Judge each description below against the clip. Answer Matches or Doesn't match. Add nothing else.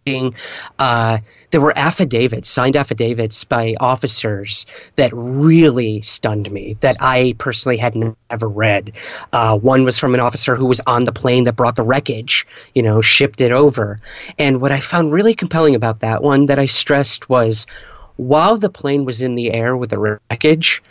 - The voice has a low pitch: Matches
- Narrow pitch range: Doesn't match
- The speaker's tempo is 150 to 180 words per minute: Matches